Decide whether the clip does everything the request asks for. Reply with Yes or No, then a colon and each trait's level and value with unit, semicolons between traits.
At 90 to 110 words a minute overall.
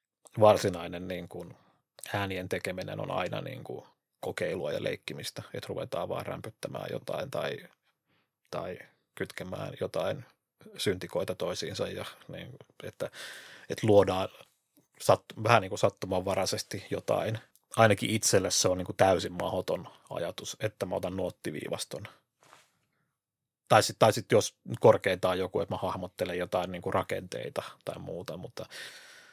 No: average, 120 wpm